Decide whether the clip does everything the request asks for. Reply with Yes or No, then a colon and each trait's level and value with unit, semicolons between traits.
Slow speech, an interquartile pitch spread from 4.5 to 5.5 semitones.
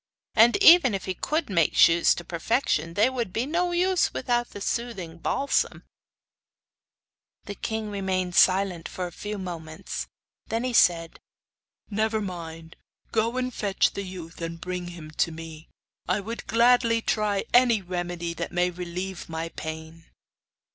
No: average, 150 wpm; average, 5.2 semitones